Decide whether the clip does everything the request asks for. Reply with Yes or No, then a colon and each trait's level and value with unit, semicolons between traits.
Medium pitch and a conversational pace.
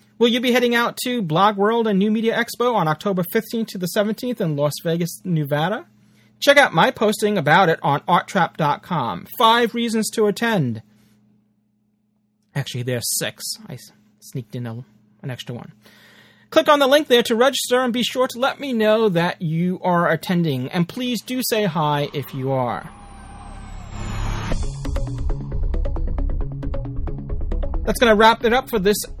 Yes: medium, 170 Hz; average, 160 wpm